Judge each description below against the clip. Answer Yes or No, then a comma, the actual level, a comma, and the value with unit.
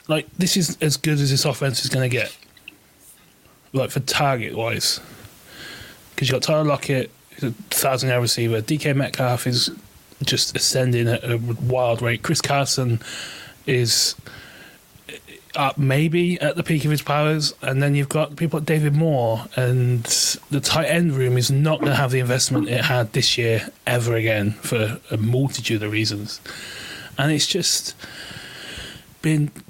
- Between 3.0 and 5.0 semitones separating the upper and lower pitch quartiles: Yes, average, 3.6 semitones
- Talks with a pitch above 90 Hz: Yes, low, 135 Hz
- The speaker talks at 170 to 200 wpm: No, average, 160 wpm